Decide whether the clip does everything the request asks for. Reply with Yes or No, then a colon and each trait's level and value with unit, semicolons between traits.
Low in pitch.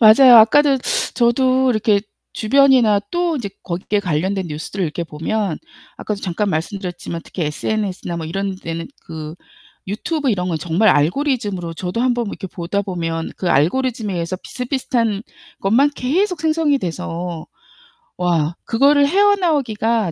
No: high, 205 Hz